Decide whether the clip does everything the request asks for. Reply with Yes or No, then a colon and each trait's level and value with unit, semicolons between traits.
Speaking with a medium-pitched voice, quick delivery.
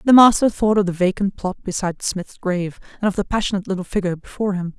No: high, 195 Hz; fast, 225 wpm